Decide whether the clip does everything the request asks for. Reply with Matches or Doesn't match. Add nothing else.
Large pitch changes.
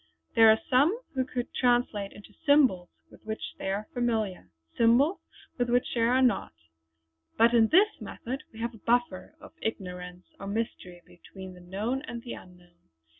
Doesn't match